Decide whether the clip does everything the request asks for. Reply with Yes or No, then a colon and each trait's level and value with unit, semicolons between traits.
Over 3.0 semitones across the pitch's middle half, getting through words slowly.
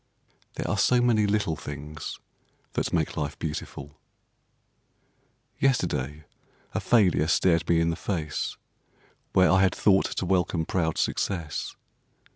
Yes: average, 3.9 semitones; slow, 125 wpm